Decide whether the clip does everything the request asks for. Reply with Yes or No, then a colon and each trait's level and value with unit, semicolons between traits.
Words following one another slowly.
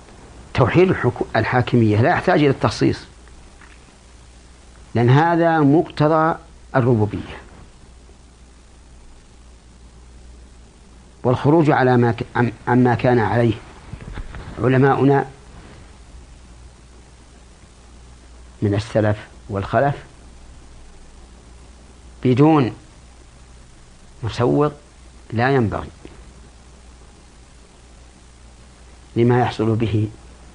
Yes: slow, 55 wpm